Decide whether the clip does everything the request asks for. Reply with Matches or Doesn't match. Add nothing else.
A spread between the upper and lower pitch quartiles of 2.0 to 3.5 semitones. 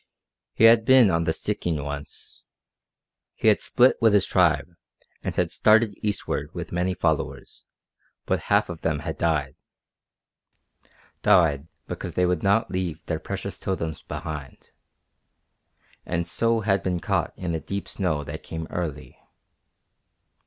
Doesn't match